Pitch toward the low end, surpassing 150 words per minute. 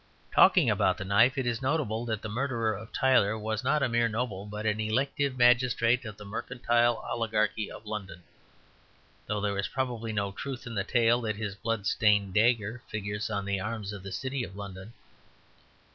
Yes: low, 110 Hz; average, 190 wpm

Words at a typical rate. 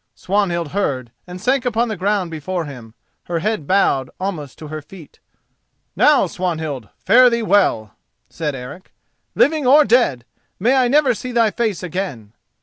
Yes: average, 155 wpm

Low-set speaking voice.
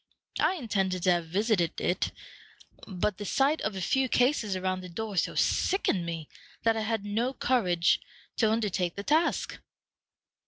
No: high, 205 Hz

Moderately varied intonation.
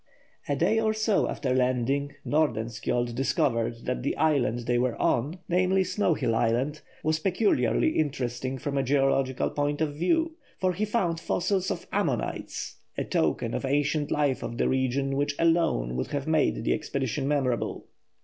Yes: average, 4.5 semitones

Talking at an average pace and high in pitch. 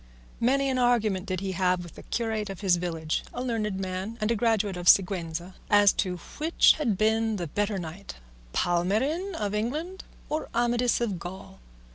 Yes: average, 175 wpm; high, 205 Hz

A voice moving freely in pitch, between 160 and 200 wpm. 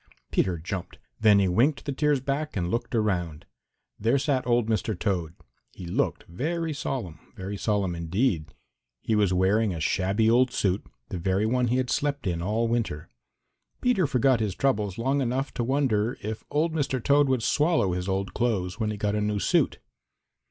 Yes: wide, 5.8 semitones; average, 180 wpm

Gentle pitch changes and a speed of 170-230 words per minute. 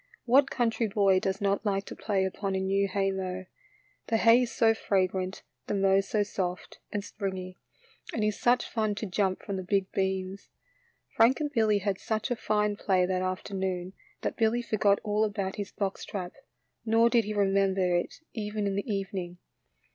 Yes: narrow, 2.1 semitones; average, 185 wpm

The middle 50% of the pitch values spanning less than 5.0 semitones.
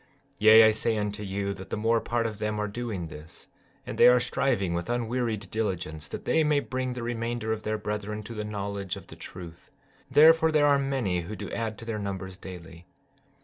Yes: average, 3.3 semitones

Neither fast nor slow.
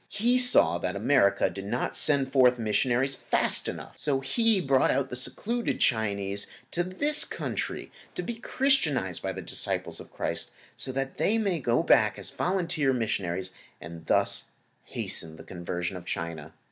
Yes: average, 160 wpm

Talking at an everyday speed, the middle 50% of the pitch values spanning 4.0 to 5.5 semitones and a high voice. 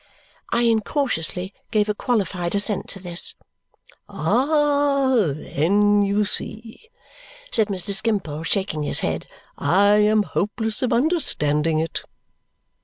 No: slow, 110 wpm; average, 4.6 semitones; high, 205 Hz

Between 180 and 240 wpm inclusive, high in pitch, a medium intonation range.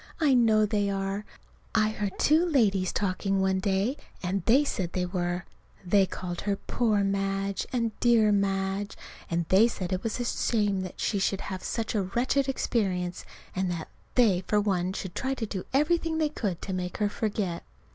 Yes: average, 185 wpm; high, 200 Hz; average, 3.2 semitones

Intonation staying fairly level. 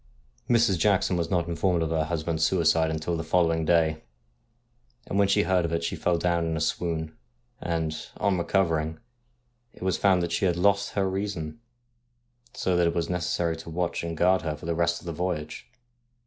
Yes: narrow, 1.9 semitones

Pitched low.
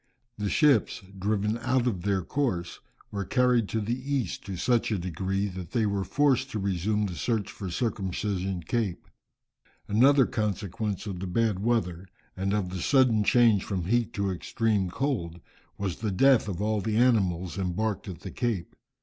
Yes: low, 105 Hz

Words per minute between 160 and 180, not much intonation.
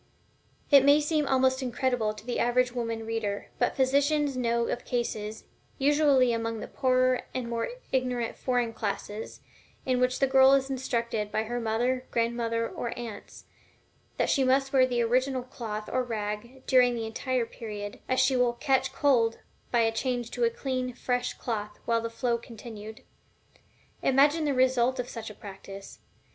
Yes: average, 165 wpm; narrow, 2.3 semitones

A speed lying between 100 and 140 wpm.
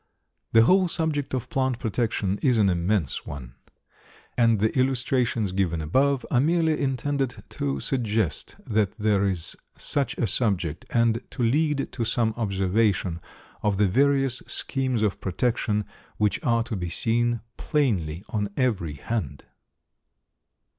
Yes: slow, 135 wpm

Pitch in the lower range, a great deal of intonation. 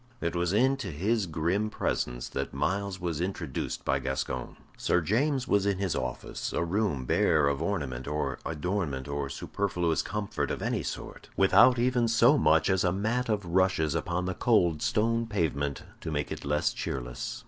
Yes: very low, 90 Hz; wide, 5.7 semitones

